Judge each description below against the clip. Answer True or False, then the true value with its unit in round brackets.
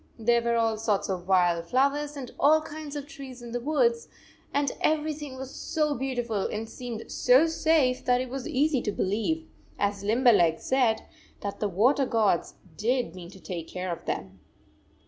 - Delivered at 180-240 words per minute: True (185 wpm)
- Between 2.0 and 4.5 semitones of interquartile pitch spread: False (5.6 semitones)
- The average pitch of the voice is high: True (245 Hz)